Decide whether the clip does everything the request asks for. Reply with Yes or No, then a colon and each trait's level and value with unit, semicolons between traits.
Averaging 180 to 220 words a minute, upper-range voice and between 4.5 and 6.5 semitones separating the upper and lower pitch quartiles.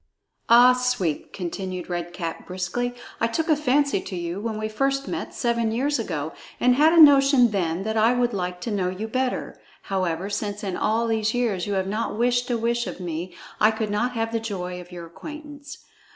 Yes: fast, 205 wpm; high, 220 Hz; average, 5.0 semitones